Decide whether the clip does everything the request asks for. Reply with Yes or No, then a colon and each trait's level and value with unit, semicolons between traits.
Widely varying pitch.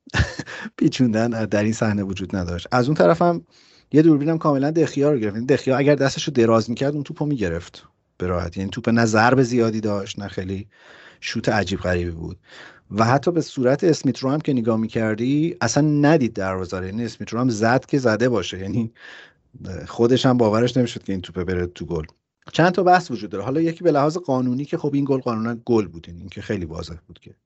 Yes: wide, 5.8 semitones